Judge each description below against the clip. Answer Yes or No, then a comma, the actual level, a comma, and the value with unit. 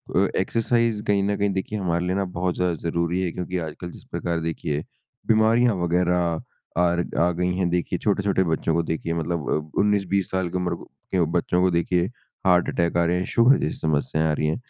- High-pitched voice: No, very low, 90 Hz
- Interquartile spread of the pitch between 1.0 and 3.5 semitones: Yes, narrow, 2.4 semitones